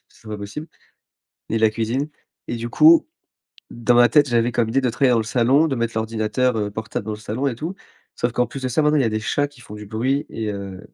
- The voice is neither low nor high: No, low, 120 Hz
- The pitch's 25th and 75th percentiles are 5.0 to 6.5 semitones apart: No, average, 3.5 semitones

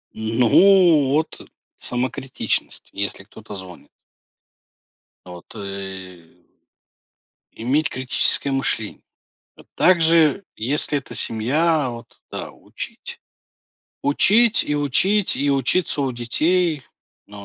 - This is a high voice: No, low, 135 Hz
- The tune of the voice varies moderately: No, wide, 6.5 semitones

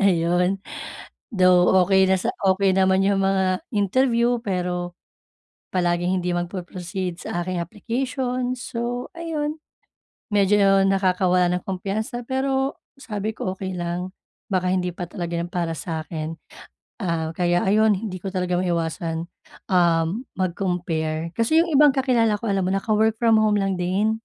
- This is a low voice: No, high, 190 Hz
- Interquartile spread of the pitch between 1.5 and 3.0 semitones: No, average, 3.6 semitones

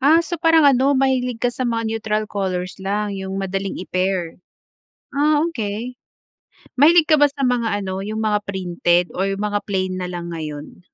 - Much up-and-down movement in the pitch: Yes, wide, 5.7 semitones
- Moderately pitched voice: No, high, 210 Hz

